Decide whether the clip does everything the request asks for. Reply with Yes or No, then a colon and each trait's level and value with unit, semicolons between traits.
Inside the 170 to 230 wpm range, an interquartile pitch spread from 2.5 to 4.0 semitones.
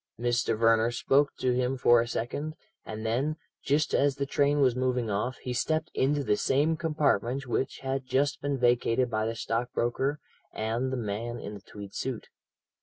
Yes: average, 180 wpm; average, 3.2 semitones